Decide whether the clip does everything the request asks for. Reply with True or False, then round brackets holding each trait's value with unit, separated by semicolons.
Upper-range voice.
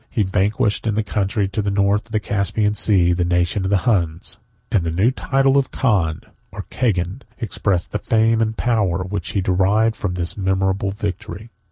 False (100 Hz)